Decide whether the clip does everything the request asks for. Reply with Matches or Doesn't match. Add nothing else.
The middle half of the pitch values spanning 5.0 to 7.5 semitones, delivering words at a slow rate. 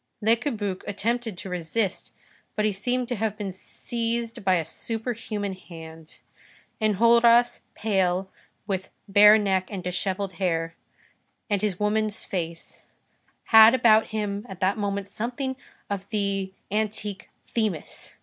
Doesn't match